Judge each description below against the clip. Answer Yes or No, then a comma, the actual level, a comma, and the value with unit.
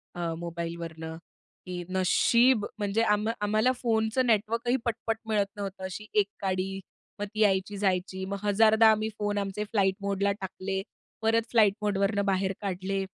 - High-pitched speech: Yes, high, 200 Hz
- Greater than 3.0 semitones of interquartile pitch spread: No, narrow, 2.5 semitones